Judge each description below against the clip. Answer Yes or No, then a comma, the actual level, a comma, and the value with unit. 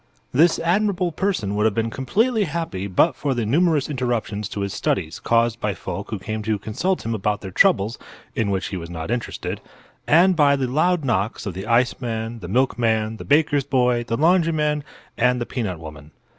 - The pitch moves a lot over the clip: Yes, wide, 6.4 semitones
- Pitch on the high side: No, low, 120 Hz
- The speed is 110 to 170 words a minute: No, average, 190 wpm